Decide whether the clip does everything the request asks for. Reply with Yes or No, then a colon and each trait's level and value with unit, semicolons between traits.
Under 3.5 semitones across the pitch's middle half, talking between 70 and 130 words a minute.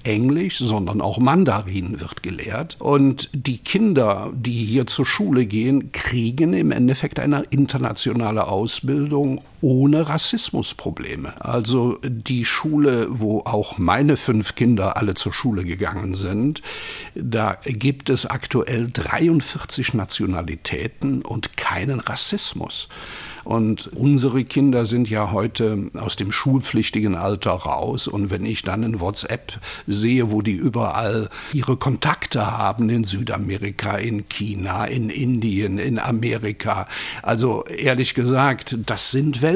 No: average, 4.4 semitones; slow, 125 wpm